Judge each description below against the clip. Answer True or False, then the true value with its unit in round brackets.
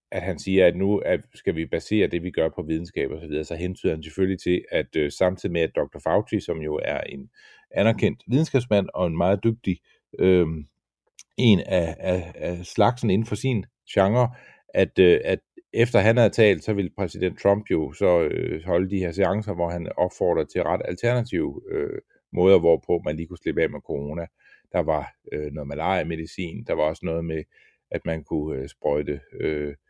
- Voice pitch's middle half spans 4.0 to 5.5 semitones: True (4.8 semitones)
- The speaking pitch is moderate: False (95 Hz)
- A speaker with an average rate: True (200 wpm)